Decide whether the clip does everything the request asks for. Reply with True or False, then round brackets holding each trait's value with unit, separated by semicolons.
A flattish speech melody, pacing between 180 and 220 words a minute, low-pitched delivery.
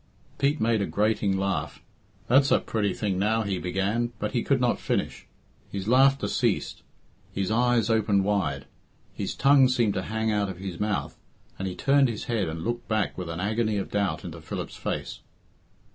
False (3.4 semitones; 185 wpm; 105 Hz)